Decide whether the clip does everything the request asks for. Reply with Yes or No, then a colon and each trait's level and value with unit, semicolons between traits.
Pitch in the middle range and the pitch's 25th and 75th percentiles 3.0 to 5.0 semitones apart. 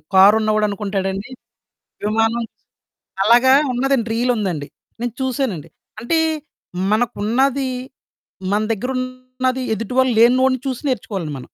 No: high, 235 Hz; average, 3.5 semitones